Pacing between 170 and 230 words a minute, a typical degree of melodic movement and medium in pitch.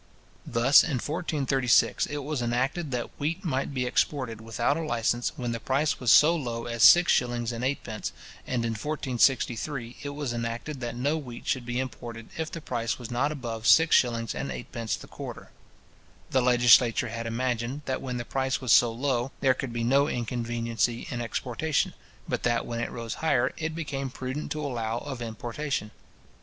No: average, 180 wpm; average, 3.1 semitones; low, 125 Hz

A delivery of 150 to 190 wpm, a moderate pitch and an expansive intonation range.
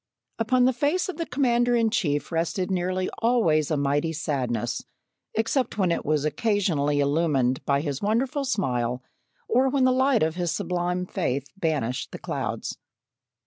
Yes: average, 155 wpm; medium, 180 Hz; wide, 8.5 semitones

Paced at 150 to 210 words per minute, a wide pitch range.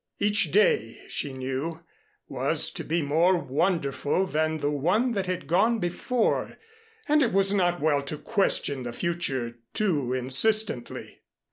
No: average, 140 wpm; wide, 5.9 semitones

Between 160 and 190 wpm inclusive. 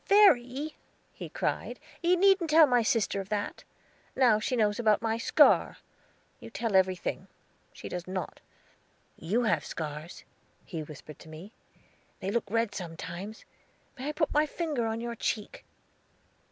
No: average, 150 wpm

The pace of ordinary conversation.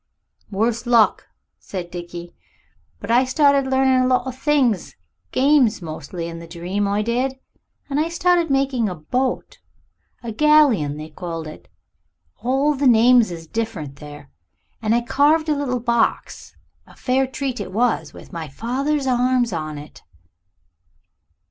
Yes: average, 150 wpm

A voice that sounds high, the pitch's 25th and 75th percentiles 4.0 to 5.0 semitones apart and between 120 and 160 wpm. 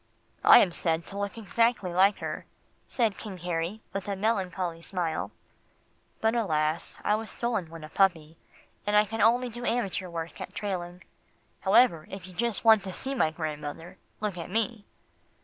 No: high, 195 Hz; average, 4.7 semitones; average, 170 wpm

